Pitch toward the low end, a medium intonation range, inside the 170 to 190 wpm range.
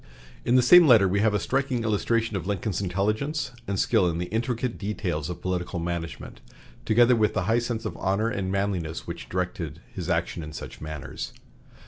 Yes: low, 100 Hz; average, 4.6 semitones; average, 185 wpm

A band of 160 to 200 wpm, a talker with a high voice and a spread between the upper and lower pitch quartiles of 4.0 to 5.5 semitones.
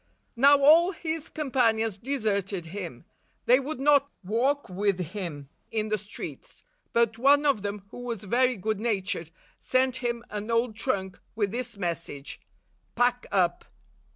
No: average, 145 wpm; high, 225 Hz; average, 4.6 semitones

